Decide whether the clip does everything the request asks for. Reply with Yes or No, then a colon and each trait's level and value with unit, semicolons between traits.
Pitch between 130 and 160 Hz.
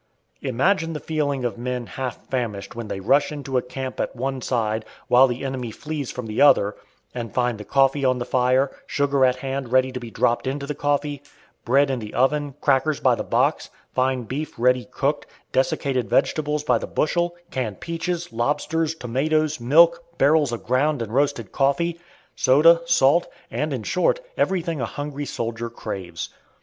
Yes: low, 135 Hz